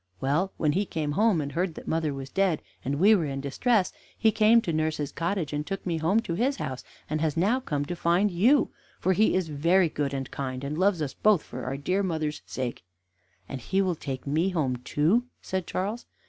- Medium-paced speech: No, fast, 220 wpm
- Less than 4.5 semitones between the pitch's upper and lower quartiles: No, average, 5.1 semitones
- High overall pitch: No, medium, 165 Hz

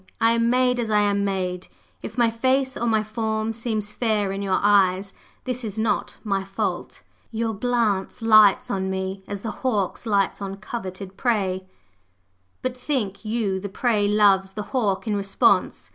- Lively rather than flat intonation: No, average, 2.9 semitones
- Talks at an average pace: Yes, average, 170 wpm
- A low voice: No, high, 210 Hz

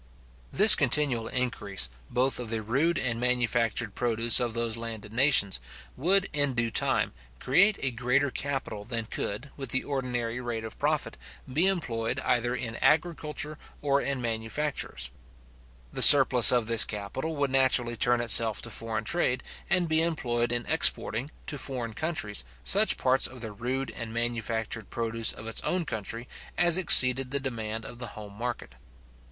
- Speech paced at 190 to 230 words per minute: No, average, 160 wpm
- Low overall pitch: Yes, low, 120 Hz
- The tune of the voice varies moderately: Yes, average, 3.3 semitones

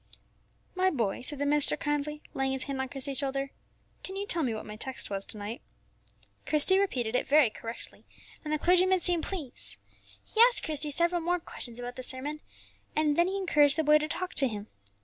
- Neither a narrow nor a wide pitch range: Yes, average, 4.8 semitones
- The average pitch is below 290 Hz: No, very high, 295 Hz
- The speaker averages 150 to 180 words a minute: No, fast, 205 wpm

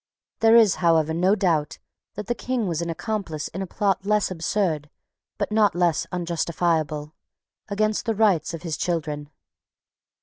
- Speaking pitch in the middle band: Yes, medium, 175 Hz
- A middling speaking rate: Yes, average, 155 wpm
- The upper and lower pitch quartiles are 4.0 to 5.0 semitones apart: Yes, average, 4.5 semitones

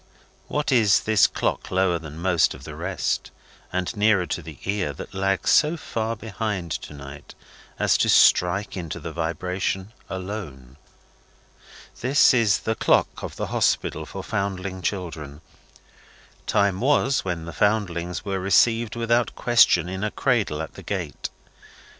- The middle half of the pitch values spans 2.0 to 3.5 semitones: No, average, 4.3 semitones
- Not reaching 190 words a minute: Yes, average, 145 wpm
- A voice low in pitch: Yes, very low, 95 Hz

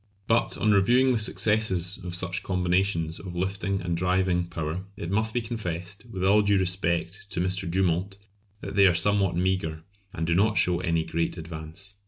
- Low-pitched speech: Yes, very low, 95 Hz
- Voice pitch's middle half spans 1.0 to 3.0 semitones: Yes, average, 2.7 semitones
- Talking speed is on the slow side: No, average, 180 wpm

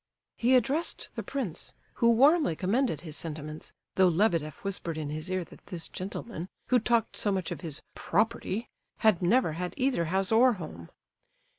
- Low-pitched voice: No, high, 190 Hz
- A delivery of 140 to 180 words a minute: Yes, average, 165 wpm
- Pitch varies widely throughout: Yes, wide, 6.1 semitones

